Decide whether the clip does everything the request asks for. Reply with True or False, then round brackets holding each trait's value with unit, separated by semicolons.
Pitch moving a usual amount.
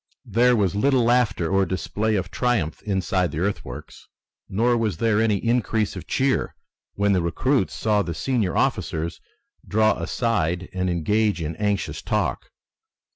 True (4.0 semitones)